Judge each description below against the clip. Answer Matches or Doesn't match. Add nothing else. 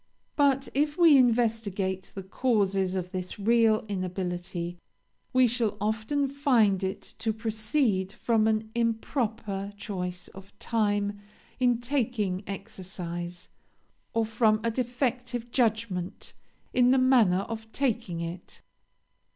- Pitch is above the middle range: Matches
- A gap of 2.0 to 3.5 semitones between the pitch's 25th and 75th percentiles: Doesn't match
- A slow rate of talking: Matches